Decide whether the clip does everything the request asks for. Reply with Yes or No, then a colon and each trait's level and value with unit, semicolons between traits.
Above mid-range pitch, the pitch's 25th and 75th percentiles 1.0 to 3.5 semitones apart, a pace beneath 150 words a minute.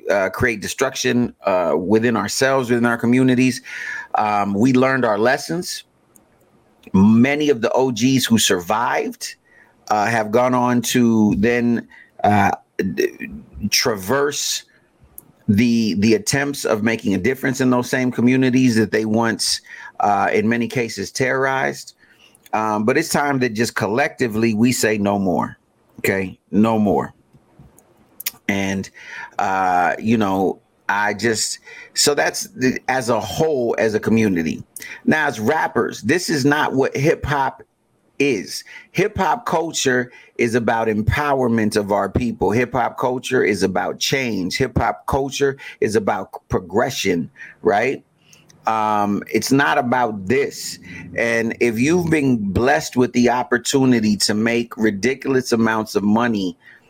No: low, 120 Hz; average, 3.2 semitones; slow, 135 wpm